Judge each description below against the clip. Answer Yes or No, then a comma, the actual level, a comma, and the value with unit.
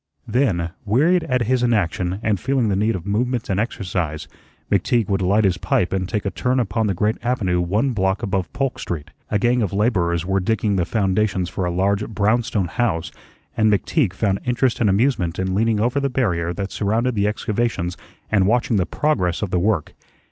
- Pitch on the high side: No, low, 105 Hz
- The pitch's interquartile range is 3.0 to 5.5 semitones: Yes, average, 4.2 semitones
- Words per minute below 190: No, average, 195 wpm